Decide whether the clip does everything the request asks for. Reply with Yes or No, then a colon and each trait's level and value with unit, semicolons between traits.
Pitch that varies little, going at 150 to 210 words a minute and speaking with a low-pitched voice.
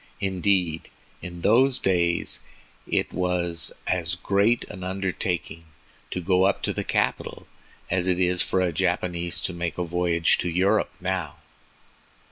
No: narrow, 1.5 semitones; average, 140 wpm; very low, 90 Hz